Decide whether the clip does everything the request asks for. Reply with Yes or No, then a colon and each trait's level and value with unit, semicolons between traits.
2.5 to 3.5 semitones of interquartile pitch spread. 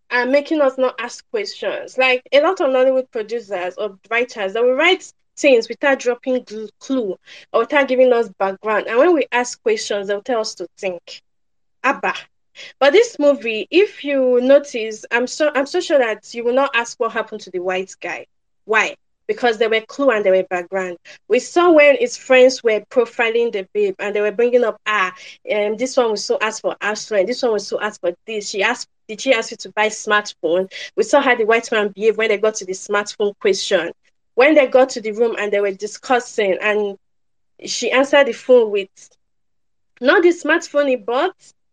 No: average, 4.2 semitones